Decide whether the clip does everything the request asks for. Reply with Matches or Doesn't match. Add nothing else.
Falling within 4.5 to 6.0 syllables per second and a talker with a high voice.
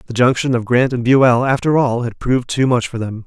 Doesn't match